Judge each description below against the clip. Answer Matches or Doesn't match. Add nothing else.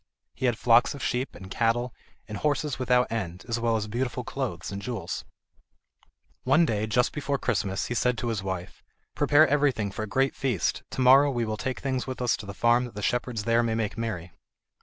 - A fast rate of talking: Matches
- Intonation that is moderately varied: Matches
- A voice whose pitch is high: Doesn't match